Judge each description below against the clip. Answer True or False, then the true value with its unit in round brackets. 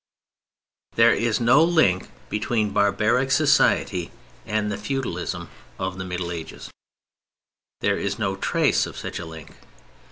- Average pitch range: True (4.3 semitones)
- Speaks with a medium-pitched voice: False (105 Hz)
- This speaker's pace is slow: True (130 wpm)